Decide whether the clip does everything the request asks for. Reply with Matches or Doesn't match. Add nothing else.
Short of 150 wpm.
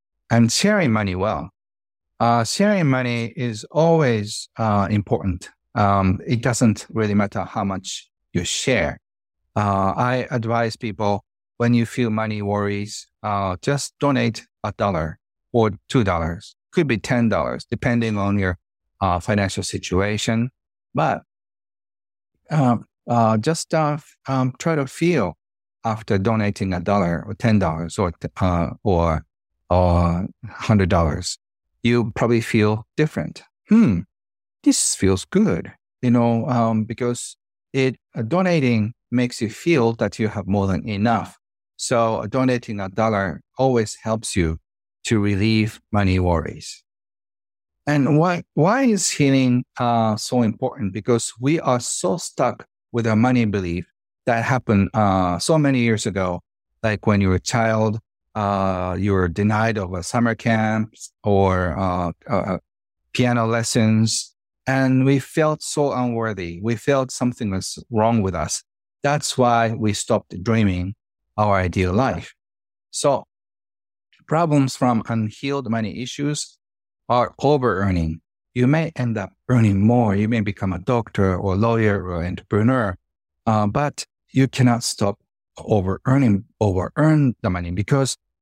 Matches